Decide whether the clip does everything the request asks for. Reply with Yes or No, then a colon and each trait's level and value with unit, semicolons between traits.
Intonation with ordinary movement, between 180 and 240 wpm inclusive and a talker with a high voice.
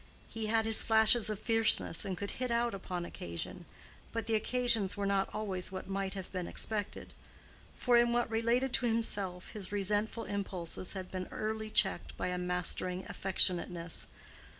No: average, 3.4 semitones; average, 165 wpm; high, 205 Hz